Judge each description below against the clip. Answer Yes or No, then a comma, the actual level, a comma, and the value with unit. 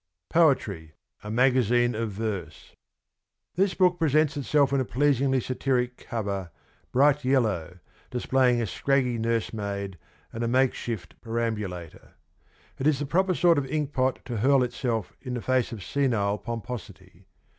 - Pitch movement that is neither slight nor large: Yes, average, 4.0 semitones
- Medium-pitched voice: No, low, 125 Hz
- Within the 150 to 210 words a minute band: No, average, 140 wpm